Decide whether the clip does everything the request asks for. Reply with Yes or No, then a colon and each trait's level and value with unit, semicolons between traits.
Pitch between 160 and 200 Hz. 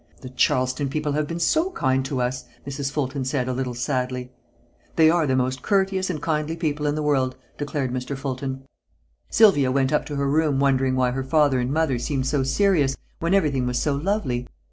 No: medium, 140 Hz